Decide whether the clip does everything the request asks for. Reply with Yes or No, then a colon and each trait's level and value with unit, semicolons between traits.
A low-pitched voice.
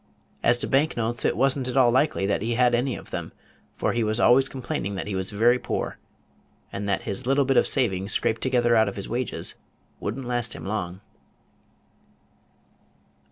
Yes: low, 120 Hz